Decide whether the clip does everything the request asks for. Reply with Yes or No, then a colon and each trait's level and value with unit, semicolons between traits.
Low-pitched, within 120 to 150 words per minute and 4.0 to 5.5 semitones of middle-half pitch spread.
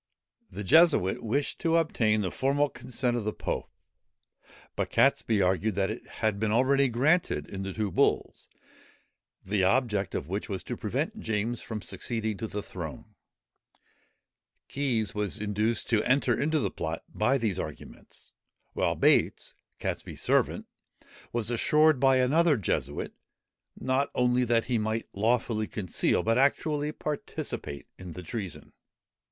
Yes: low, 115 Hz; average, 145 wpm; average, 4.5 semitones